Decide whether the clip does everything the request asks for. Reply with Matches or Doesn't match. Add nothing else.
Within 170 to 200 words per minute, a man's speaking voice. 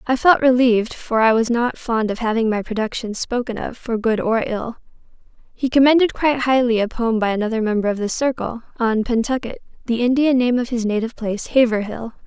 Doesn't match